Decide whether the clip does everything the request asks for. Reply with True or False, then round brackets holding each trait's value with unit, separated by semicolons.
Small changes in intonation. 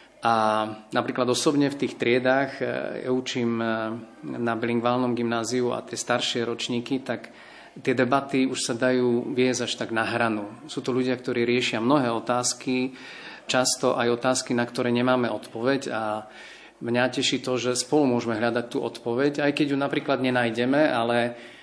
True (1.5 semitones)